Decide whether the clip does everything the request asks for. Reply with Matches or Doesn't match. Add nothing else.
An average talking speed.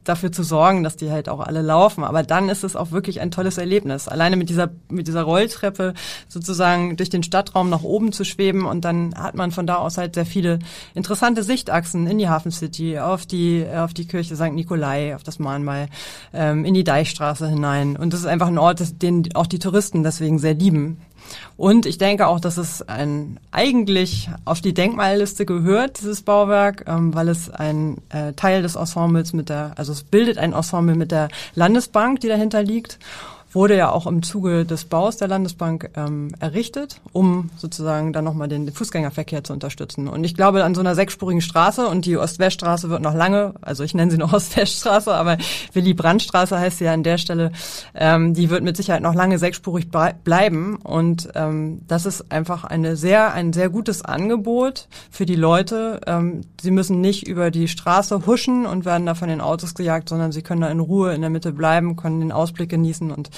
Doesn't match